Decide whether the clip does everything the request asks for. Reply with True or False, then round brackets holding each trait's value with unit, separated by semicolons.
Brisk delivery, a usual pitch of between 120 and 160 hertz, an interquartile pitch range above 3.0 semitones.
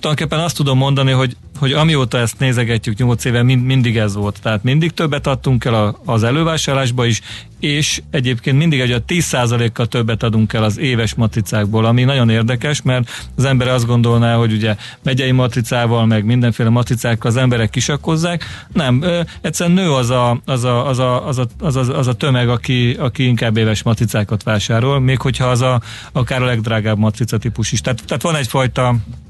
False (160 wpm; 125 Hz; 2.6 semitones)